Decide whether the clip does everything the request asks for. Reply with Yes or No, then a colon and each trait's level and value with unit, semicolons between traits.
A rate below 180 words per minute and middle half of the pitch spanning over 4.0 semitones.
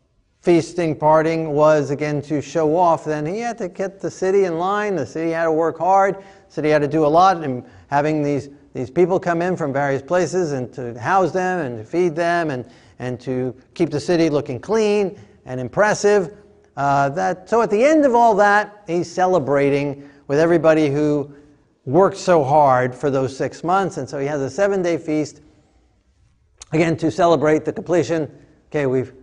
No: average, 190 wpm; average, 4.5 semitones